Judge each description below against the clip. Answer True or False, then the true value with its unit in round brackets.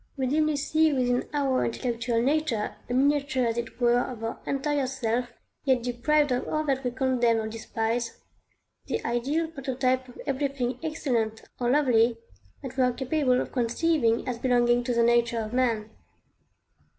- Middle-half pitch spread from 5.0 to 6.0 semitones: False (2.8 semitones)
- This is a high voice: True (250 Hz)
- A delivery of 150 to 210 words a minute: True (165 wpm)